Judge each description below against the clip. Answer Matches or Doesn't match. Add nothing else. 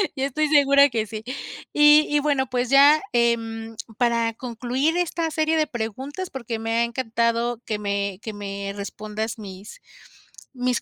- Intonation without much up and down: Doesn't match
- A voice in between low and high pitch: Doesn't match